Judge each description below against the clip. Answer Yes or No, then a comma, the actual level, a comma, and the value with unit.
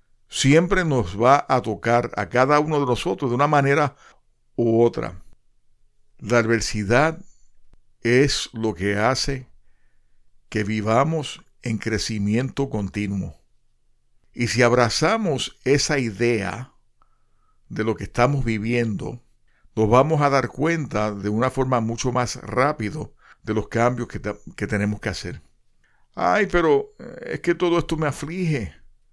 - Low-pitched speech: Yes, low, 120 Hz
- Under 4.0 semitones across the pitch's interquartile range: No, average, 4.5 semitones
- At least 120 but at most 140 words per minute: Yes, average, 130 wpm